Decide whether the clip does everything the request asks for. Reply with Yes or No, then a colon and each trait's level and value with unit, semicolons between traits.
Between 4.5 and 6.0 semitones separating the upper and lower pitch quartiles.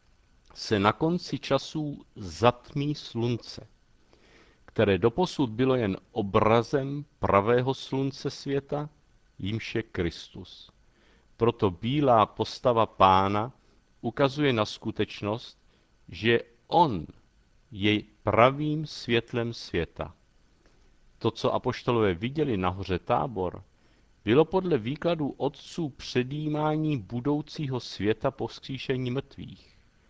Yes: average, 5.3 semitones